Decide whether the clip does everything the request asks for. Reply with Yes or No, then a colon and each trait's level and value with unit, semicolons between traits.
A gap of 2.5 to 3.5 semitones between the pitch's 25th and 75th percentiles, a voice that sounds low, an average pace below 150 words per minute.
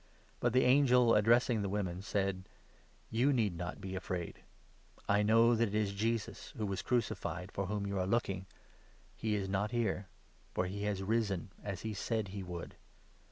No: average, 3.0 semitones; low, 105 Hz; average, 190 wpm